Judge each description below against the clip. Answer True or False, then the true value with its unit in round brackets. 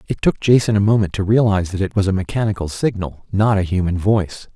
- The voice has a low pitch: True (100 Hz)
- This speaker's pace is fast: True (225 wpm)